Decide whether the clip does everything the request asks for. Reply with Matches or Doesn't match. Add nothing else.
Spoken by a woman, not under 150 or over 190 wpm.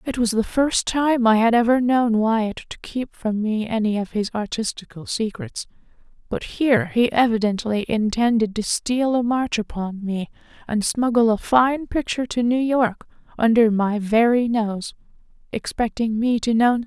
Matches